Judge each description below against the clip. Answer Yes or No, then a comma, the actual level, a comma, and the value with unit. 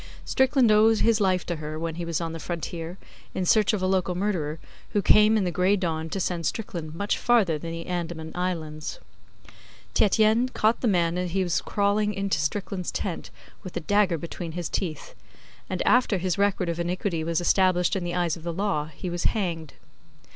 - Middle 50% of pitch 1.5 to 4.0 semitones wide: Yes, average, 3.4 semitones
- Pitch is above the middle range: No, medium, 180 Hz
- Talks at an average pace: Yes, average, 195 wpm